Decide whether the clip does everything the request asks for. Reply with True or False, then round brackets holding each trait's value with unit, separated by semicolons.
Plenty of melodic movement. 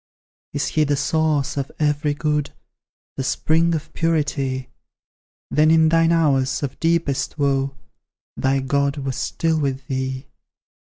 False (2.6 semitones)